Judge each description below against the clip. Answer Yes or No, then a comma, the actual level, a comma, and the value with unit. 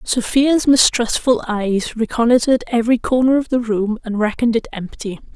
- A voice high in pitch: Yes, high, 235 Hz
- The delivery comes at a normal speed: Yes, average, 145 wpm